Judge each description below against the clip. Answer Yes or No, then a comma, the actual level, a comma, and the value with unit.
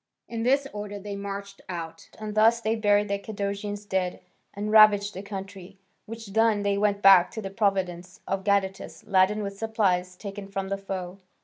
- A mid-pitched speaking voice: No, high, 200 Hz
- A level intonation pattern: Yes, narrow, 1.5 semitones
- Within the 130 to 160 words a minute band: No, average, 180 wpm